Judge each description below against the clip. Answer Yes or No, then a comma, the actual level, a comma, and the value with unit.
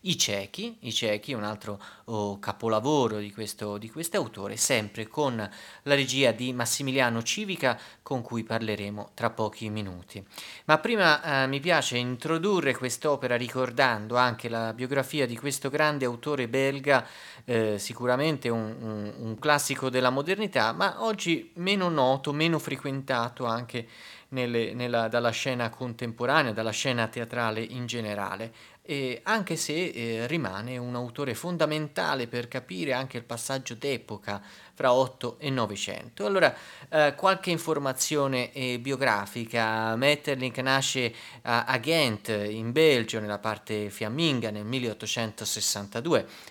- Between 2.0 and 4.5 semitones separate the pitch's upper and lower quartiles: Yes, average, 3.8 semitones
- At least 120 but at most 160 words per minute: Yes, average, 130 wpm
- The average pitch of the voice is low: Yes, low, 125 Hz